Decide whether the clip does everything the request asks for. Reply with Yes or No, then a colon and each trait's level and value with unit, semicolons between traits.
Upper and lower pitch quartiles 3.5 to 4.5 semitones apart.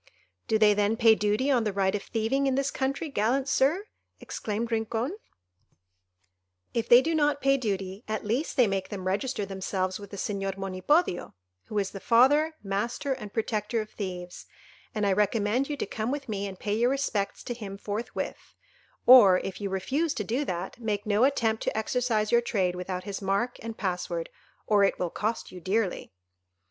Yes: average, 4.2 semitones